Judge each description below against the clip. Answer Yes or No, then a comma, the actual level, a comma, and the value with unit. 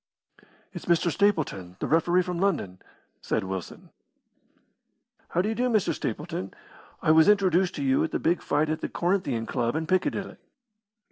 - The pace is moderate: Yes, average, 160 wpm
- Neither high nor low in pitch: Yes, medium, 170 Hz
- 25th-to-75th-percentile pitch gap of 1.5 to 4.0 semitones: No, average, 4.7 semitones